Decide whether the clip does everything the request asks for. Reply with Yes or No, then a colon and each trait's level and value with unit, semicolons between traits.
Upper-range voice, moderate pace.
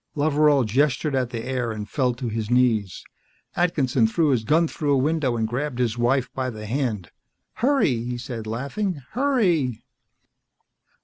No: low, 130 Hz; average, 160 wpm